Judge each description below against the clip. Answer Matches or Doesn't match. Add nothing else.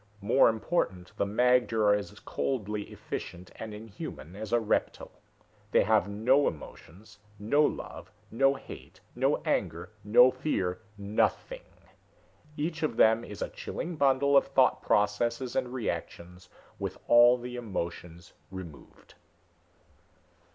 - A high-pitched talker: Doesn't match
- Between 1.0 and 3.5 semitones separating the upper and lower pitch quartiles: Doesn't match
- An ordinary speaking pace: Doesn't match